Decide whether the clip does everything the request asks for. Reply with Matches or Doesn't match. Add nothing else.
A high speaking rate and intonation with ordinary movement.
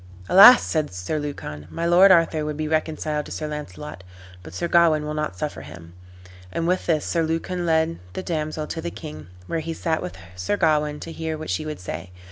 Doesn't match